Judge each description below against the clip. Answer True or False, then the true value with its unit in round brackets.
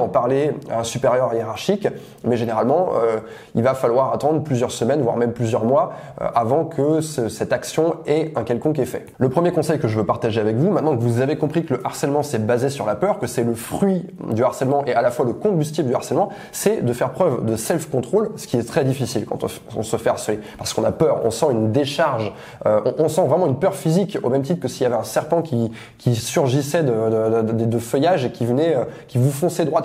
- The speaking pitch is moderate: False (130 Hz)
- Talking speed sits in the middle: False (250 wpm)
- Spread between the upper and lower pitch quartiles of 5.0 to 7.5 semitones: True (5.3 semitones)